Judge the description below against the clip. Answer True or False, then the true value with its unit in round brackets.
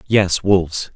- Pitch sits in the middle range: False (95 Hz)